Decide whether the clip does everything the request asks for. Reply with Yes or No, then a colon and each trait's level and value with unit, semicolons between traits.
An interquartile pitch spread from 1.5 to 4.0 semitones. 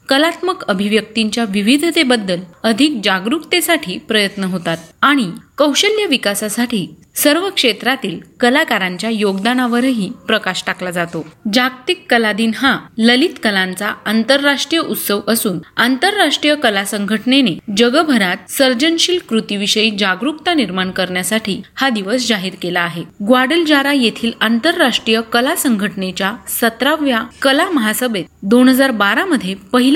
No: average, 5.3 semitones